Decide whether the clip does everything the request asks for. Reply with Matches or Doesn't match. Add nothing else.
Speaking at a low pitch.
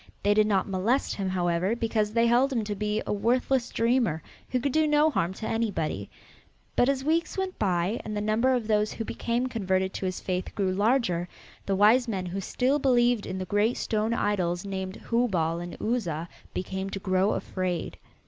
Doesn't match